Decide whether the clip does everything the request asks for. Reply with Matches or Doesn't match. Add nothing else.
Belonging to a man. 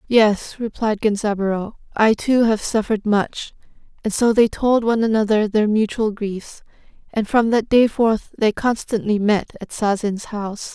Doesn't match